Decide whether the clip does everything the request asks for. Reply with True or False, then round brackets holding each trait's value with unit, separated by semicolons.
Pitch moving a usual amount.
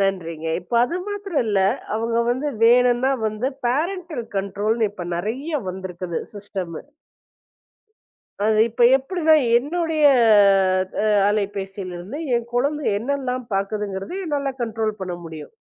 False (6.2 semitones)